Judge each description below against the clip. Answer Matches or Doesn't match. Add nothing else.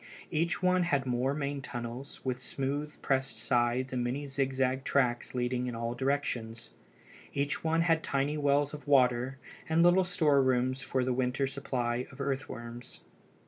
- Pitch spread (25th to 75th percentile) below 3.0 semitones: Matches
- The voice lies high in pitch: Doesn't match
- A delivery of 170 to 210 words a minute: Doesn't match